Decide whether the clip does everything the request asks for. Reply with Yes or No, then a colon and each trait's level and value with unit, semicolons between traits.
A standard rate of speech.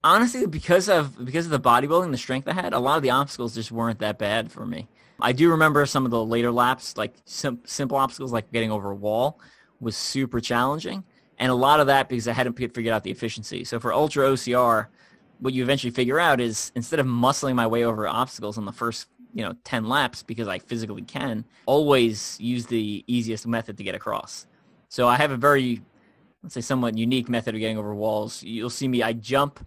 No: fast, 220 wpm